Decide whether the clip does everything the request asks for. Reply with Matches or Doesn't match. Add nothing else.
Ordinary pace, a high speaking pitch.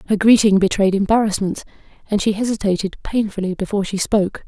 Matches